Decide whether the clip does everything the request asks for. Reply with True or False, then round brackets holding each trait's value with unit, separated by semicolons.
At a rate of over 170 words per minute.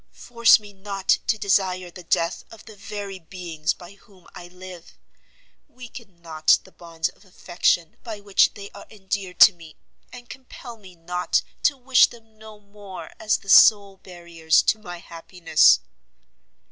False (160 wpm)